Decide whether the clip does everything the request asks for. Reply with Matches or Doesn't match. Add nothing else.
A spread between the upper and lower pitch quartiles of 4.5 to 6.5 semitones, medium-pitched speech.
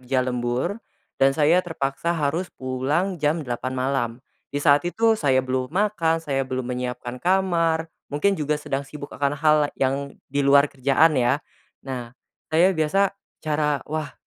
Doesn't match